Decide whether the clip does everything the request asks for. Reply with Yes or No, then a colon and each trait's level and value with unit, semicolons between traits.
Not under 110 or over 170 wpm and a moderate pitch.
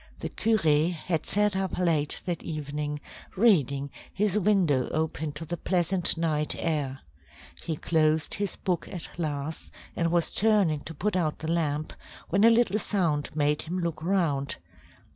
Yes: average, 155 wpm; medium, 165 Hz